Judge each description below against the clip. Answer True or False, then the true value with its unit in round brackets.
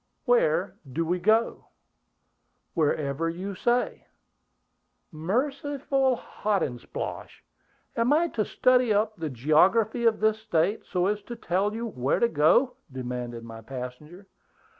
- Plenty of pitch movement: True (7.5 semitones)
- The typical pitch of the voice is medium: False (200 Hz)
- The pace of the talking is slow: True (120 wpm)